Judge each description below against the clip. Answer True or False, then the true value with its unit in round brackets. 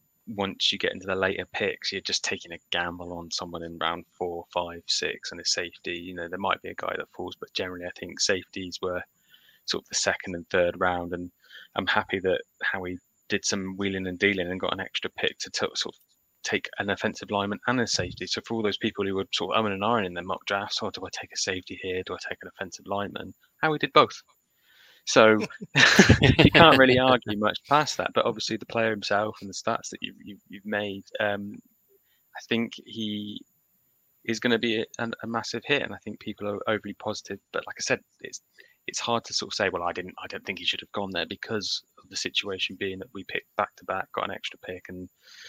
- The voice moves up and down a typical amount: True (3.2 semitones)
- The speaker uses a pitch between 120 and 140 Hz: False (100 Hz)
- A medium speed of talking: False (240 wpm)